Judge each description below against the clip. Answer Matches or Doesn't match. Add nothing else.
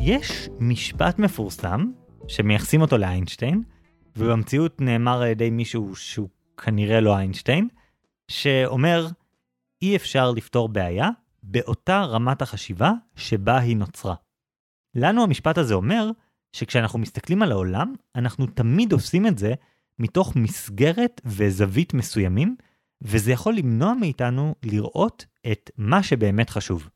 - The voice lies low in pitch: Matches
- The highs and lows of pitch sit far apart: Matches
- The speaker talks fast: Doesn't match